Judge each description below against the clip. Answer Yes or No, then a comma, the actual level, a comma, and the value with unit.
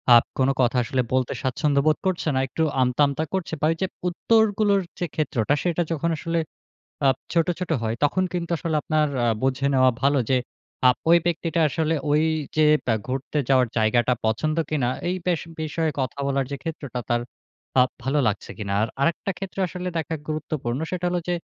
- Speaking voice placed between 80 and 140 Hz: No, medium, 150 Hz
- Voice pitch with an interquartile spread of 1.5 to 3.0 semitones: No, average, 4.3 semitones